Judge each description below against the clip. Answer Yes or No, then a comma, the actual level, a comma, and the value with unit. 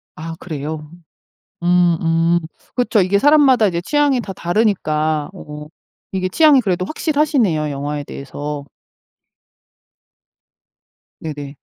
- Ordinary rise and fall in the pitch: No, wide, 6.4 semitones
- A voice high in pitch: No, medium, 175 Hz